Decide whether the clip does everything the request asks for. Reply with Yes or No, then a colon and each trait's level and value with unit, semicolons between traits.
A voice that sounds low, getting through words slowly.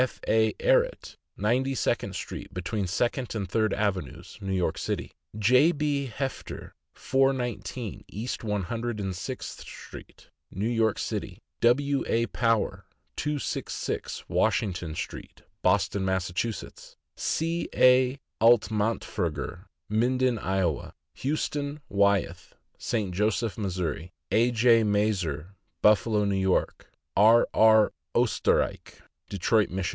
Yes: low, 110 Hz; slow, 110 wpm